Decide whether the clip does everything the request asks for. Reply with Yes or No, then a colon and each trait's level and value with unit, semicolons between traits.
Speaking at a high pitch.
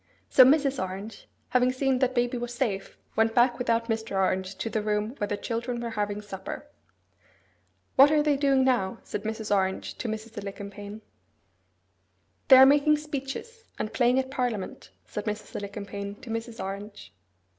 Yes: high, 225 Hz